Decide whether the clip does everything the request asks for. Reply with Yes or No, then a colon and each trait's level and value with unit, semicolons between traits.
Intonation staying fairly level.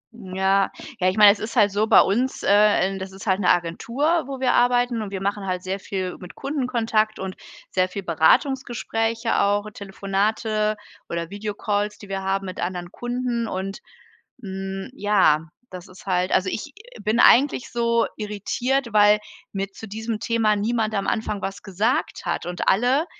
No: average, 3.1 semitones